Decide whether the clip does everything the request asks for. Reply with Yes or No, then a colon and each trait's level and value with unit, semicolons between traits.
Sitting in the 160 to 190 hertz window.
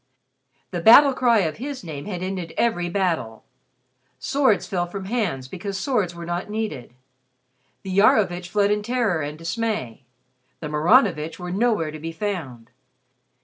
Yes: medium, 185 Hz